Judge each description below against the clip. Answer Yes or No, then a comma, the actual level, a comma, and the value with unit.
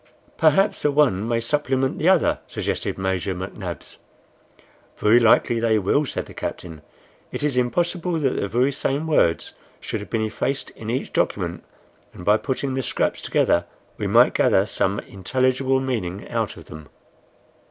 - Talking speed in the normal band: Yes, average, 160 wpm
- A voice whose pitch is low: Yes, low, 120 Hz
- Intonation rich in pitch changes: Yes, wide, 5.7 semitones